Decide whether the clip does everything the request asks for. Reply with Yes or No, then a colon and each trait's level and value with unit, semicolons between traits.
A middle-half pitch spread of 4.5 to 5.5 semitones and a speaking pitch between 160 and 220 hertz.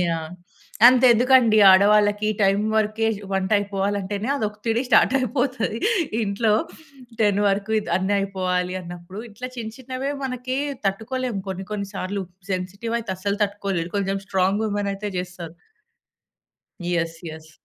No: average, 2.8 semitones; high, 205 Hz